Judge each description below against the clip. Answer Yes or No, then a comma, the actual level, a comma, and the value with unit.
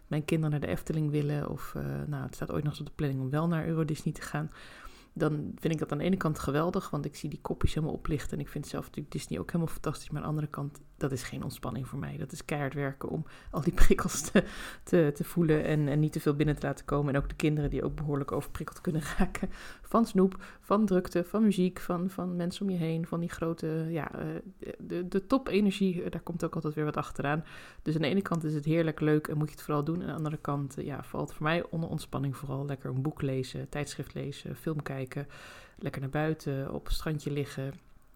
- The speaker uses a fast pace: Yes, fast, 250 wpm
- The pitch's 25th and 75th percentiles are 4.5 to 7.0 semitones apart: No, average, 2.9 semitones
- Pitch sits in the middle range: Yes, medium, 155 Hz